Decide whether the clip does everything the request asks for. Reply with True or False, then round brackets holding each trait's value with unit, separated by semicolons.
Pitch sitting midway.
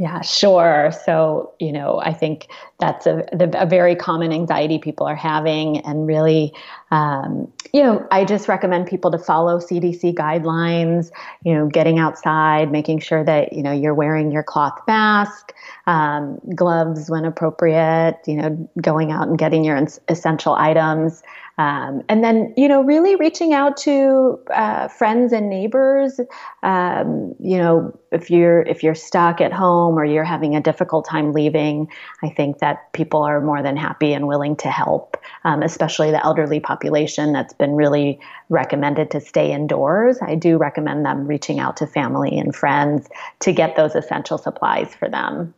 True (160 Hz)